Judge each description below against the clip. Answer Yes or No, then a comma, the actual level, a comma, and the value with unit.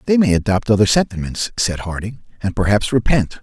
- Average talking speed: Yes, average, 175 wpm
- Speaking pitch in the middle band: No, low, 110 Hz